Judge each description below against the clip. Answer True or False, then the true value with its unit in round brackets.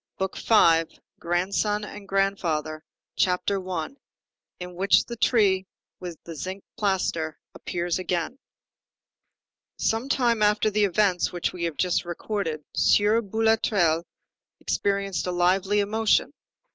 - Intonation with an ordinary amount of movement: True (3.1 semitones)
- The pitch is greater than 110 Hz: True (190 Hz)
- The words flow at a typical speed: False (110 wpm)